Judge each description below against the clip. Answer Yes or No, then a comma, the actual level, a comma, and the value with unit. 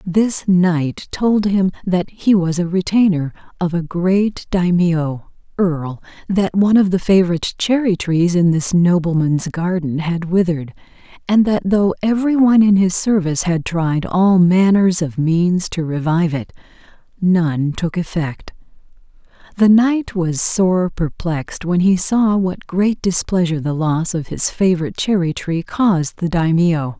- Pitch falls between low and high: Yes, medium, 180 Hz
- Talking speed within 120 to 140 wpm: No, average, 150 wpm